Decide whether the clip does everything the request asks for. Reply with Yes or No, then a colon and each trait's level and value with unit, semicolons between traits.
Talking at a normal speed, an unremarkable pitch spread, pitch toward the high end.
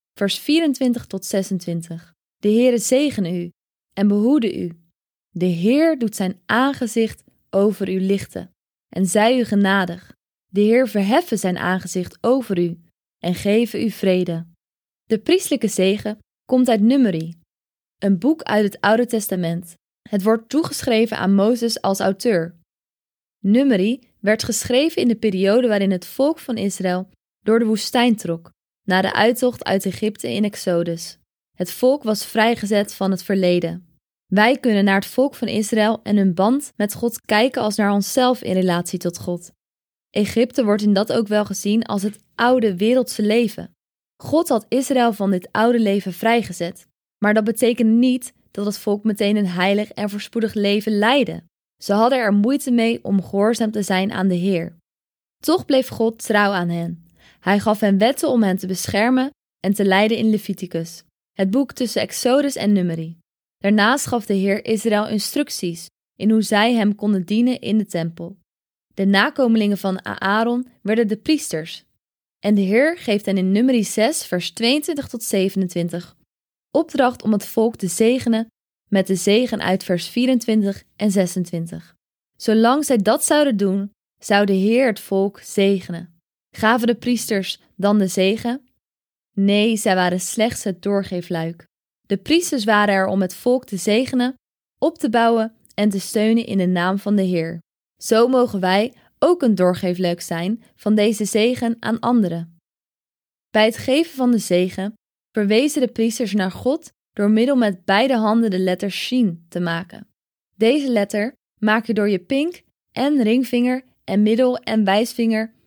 Yes: average, 160 wpm; average, 3.7 semitones; high, 210 Hz